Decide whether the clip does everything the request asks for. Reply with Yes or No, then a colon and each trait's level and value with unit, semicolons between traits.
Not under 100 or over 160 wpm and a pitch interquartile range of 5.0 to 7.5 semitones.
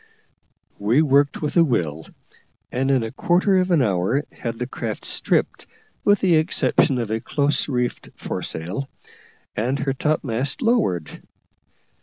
Yes: average, 140 wpm; wide, 5.5 semitones